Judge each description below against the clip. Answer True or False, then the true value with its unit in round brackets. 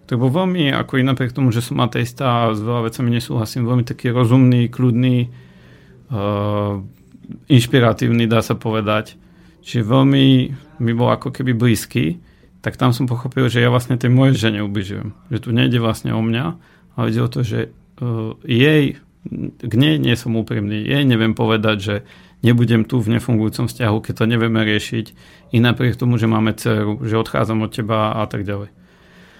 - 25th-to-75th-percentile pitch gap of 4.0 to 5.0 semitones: False (2.6 semitones)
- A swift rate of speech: True (175 wpm)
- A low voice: True (120 Hz)